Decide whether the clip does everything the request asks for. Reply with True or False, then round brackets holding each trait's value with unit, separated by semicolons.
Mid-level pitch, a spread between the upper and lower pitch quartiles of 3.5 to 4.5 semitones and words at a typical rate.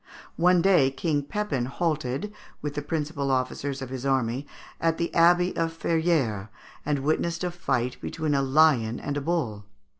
True (145 Hz; 4.0 semitones; 160 wpm)